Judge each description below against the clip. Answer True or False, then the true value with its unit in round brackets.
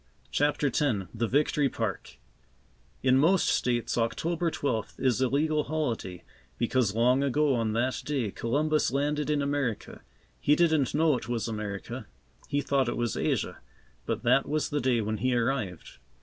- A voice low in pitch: True (130 Hz)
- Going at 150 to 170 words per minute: True (160 wpm)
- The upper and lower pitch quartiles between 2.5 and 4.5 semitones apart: True (4.2 semitones)